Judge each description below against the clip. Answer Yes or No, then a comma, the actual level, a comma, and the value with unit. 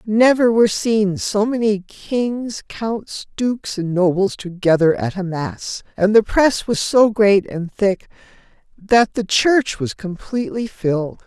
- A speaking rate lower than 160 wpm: Yes, average, 150 wpm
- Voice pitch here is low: No, high, 210 Hz